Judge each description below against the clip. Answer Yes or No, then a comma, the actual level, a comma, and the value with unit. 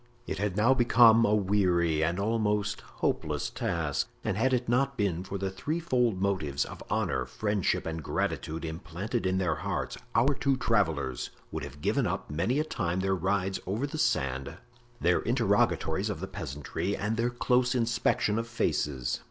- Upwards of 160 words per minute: Yes, average, 170 wpm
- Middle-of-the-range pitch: No, low, 100 Hz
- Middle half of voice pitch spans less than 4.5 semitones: No, wide, 5.6 semitones